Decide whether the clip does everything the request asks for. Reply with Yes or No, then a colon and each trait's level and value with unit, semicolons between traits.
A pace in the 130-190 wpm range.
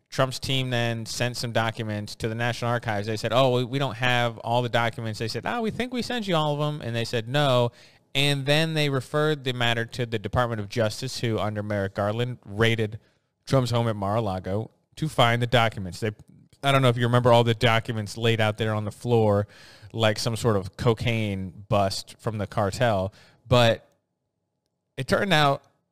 No: fast, 205 wpm